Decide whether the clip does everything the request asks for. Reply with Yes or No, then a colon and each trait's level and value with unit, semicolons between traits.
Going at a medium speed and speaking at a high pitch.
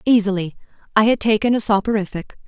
Yes: average, 145 wpm; high, 210 Hz